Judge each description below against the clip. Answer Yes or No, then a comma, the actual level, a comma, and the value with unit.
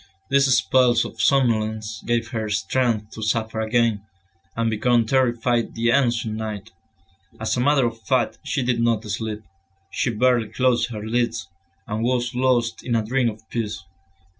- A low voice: Yes, low, 115 Hz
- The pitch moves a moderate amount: No, narrow, 2.0 semitones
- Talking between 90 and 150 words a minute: No, average, 160 wpm